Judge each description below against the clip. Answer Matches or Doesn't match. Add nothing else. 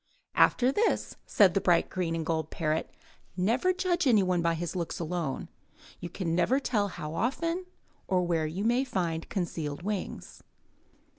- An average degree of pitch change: Doesn't match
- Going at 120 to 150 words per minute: Doesn't match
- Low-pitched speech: Doesn't match